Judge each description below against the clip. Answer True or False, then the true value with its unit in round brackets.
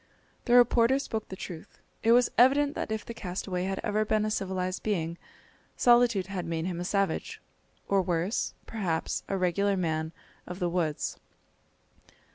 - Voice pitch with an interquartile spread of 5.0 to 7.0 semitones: False (3.8 semitones)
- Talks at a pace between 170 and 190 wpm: False (160 wpm)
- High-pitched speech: True (195 Hz)